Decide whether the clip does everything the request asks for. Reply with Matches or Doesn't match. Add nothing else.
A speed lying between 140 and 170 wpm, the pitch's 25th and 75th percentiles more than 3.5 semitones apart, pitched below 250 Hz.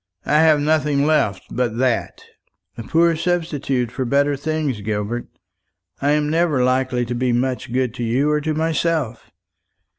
Matches